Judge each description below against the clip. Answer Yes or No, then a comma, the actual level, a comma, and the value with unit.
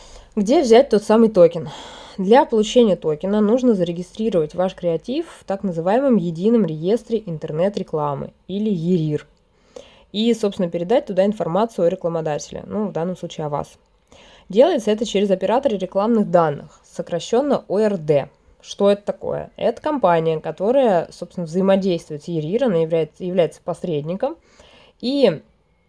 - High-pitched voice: Yes, high, 195 Hz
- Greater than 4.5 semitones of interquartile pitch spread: Yes, average, 4.9 semitones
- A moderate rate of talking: Yes, average, 130 wpm